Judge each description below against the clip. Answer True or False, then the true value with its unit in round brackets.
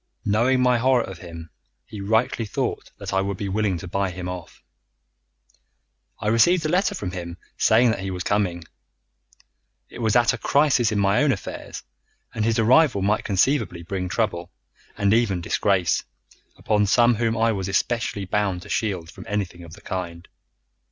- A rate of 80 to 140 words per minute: False (175 wpm)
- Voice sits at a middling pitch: False (105 Hz)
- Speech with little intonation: False (4.1 semitones)